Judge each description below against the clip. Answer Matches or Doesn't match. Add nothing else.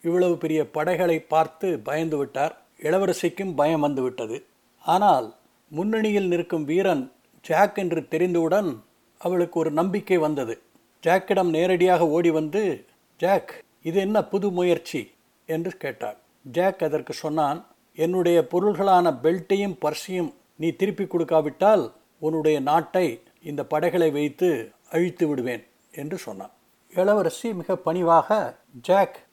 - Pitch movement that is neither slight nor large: Matches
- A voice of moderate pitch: Matches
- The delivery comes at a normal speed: Matches